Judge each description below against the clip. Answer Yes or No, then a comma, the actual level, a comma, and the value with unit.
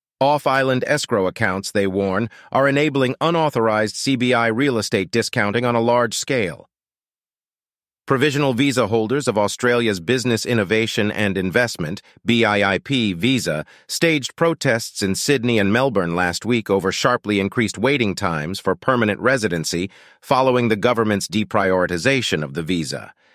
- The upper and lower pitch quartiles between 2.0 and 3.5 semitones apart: No, average, 4.8 semitones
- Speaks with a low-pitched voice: Yes, low, 115 Hz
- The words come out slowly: Yes, slow, 130 wpm